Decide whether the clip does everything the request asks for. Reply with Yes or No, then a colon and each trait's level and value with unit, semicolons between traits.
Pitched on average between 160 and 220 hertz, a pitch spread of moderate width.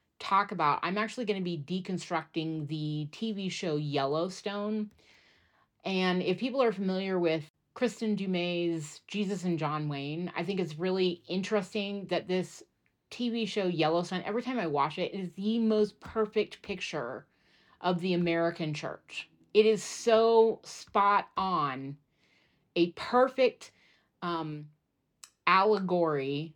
Yes: medium, 185 Hz; average, 4.4 semitones